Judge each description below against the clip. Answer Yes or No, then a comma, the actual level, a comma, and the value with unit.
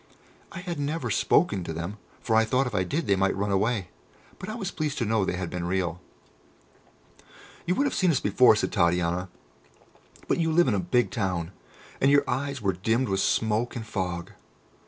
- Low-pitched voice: Yes, low, 110 Hz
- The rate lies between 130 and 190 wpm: No, average, 200 wpm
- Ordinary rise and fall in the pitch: No, wide, 7.2 semitones